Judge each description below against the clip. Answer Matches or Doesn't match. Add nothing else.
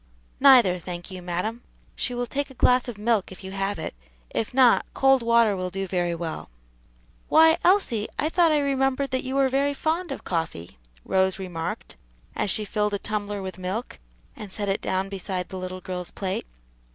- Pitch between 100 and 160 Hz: Doesn't match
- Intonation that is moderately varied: Doesn't match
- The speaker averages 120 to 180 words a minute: Doesn't match